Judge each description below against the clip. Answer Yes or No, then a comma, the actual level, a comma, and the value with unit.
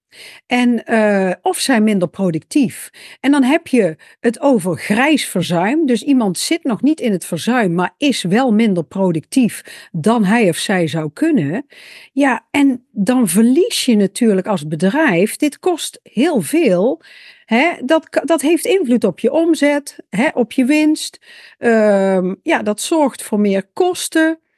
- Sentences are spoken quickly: No, average, 155 wpm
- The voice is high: Yes, high, 245 Hz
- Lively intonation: Yes, wide, 7.3 semitones